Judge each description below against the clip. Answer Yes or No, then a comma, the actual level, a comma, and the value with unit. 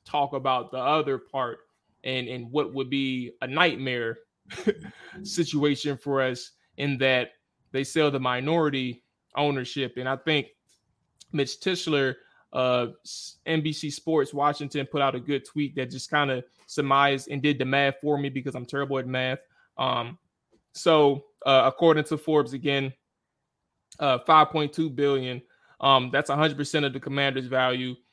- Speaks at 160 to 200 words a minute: No, average, 145 wpm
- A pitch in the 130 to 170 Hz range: Yes, medium, 140 Hz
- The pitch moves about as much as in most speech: No, narrow, 2.3 semitones